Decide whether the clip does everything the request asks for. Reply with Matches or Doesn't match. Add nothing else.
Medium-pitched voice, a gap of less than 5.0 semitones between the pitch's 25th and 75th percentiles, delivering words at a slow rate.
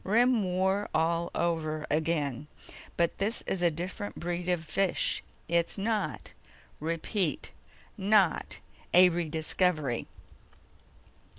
Matches